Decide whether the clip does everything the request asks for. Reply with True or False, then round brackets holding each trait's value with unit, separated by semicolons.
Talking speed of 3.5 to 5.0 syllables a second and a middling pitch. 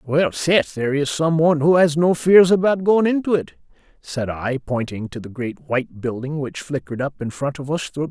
False (5.3 syllables/s; 150 Hz)